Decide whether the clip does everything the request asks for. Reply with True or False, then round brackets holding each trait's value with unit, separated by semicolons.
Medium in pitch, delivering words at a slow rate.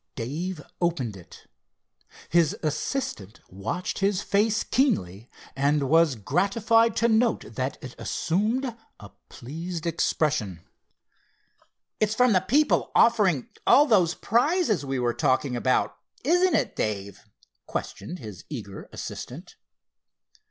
True (170 Hz; 115 wpm)